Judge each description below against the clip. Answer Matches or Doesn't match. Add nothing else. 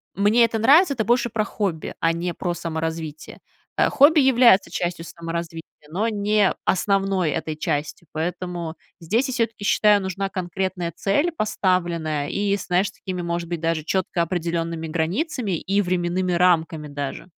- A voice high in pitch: Doesn't match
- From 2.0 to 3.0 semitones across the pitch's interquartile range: Doesn't match